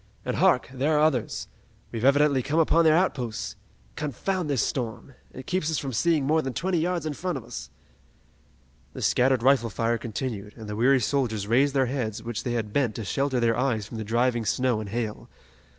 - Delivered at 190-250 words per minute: Yes, average, 200 wpm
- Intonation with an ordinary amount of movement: Yes, average, 4.3 semitones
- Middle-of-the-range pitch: No, low, 130 Hz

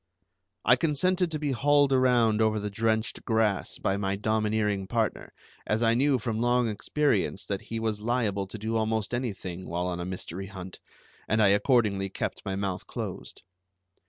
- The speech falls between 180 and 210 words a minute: No, average, 170 wpm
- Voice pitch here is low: Yes, low, 110 Hz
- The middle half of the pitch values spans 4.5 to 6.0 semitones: No, average, 3.6 semitones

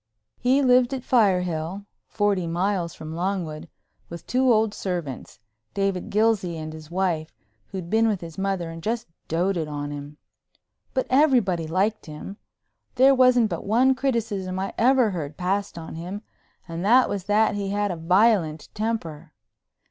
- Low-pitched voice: No, high, 195 Hz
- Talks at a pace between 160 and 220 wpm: No, average, 150 wpm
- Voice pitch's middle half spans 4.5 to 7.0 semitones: Yes, average, 4.9 semitones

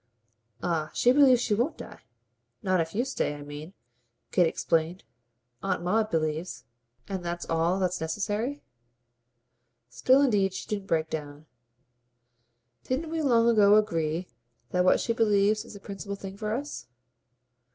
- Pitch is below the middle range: No, high, 195 Hz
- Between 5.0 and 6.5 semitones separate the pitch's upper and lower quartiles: Yes, wide, 5.4 semitones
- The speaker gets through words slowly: No, average, 145 wpm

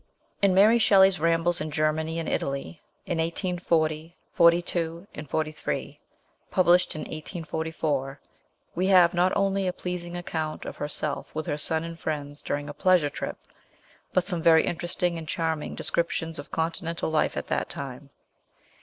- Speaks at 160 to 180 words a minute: No, average, 145 wpm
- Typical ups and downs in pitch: No, narrow, 2.2 semitones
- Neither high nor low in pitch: Yes, medium, 165 Hz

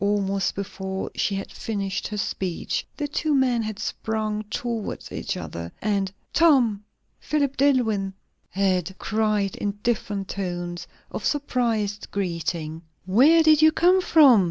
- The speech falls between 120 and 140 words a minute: Yes, slow, 135 wpm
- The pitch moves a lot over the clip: No, average, 4.6 semitones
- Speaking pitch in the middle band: No, high, 210 Hz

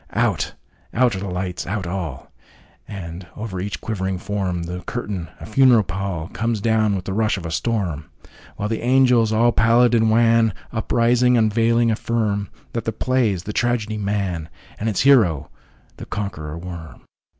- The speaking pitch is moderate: No, low, 105 Hz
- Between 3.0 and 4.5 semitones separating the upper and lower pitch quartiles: Yes, average, 4.0 semitones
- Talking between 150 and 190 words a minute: No, slow, 135 wpm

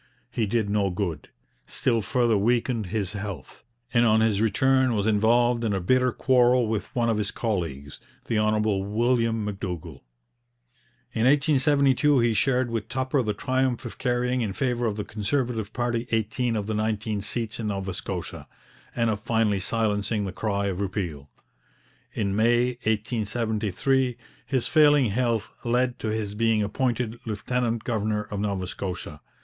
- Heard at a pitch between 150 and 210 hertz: No, low, 110 Hz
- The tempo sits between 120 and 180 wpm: Yes, average, 155 wpm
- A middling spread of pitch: Yes, average, 3.0 semitones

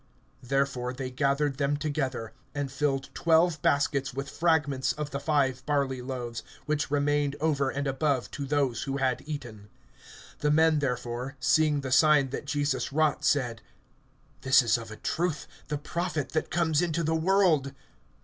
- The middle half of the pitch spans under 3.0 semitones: Yes, narrow, 2.4 semitones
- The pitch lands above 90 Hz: Yes, medium, 140 Hz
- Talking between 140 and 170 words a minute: Yes, average, 160 wpm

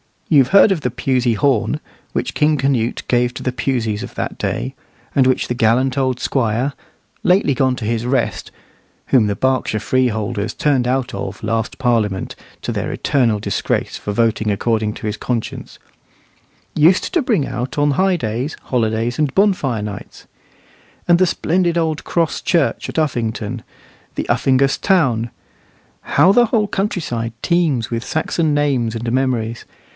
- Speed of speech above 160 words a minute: No, average, 155 wpm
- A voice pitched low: Yes, low, 130 Hz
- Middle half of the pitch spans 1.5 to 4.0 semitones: No, average, 4.7 semitones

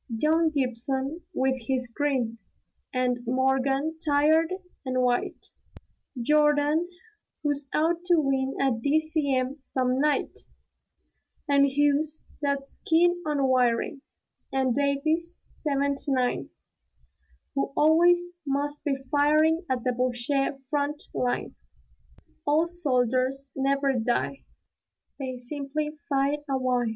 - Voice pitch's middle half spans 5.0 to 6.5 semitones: No, average, 2.7 semitones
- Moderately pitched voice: No, very high, 280 Hz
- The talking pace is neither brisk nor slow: No, slow, 105 wpm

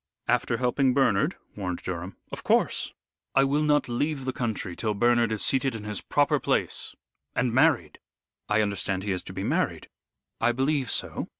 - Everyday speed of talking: Yes, average, 175 wpm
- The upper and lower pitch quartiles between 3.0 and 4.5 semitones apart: No, average, 4.9 semitones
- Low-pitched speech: Yes, low, 115 Hz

